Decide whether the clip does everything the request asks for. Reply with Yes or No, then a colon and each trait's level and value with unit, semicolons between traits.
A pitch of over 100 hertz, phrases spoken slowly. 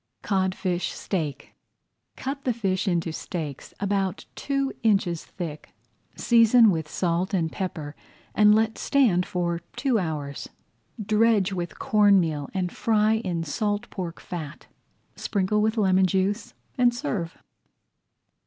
Yes: high, 190 Hz; slow, 125 wpm